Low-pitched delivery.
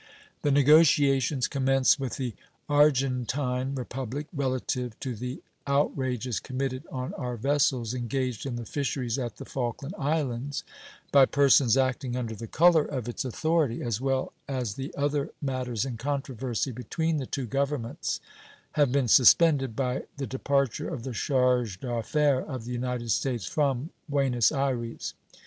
Yes: low, 130 Hz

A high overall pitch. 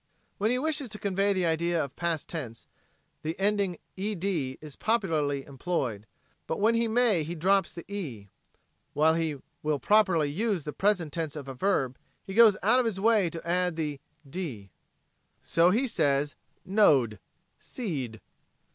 No: medium, 170 Hz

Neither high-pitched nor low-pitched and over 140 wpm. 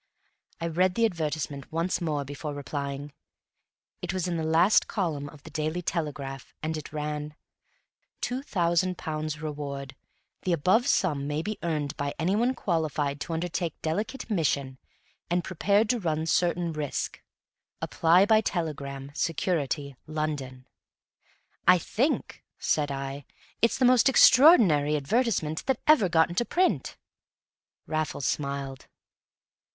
No: medium, 160 Hz; slow, 135 wpm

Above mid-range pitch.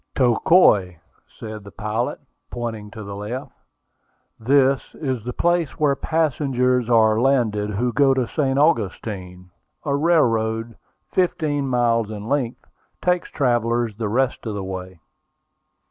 No: low, 120 Hz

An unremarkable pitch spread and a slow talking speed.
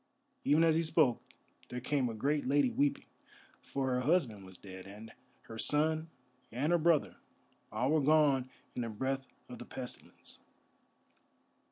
No: average, 4.5 semitones; average, 155 wpm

